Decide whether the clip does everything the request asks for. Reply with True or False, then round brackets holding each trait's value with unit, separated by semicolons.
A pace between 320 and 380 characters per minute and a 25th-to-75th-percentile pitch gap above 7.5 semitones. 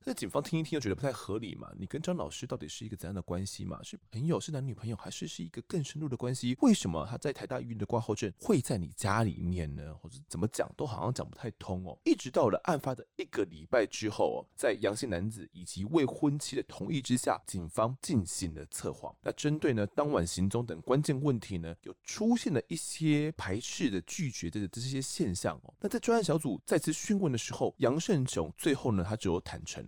True (345 characters per minute; 7.9 semitones)